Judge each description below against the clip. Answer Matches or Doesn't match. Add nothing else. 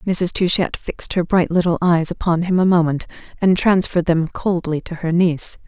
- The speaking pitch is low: Doesn't match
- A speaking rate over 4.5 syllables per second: Matches